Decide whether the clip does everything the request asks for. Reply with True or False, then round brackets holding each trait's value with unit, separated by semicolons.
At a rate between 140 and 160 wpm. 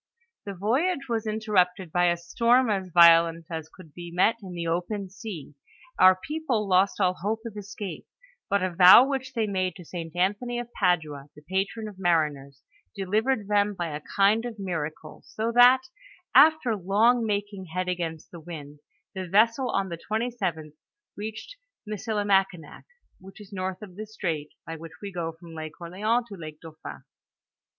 False (170 wpm)